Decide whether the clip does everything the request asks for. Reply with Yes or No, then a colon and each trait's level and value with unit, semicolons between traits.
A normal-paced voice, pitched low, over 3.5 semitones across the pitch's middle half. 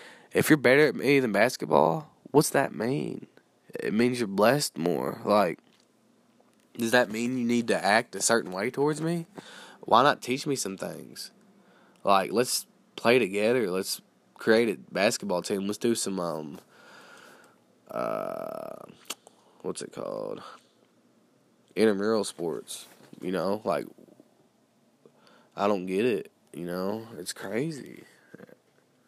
No: slow, 130 wpm; low, 110 Hz; average, 3.9 semitones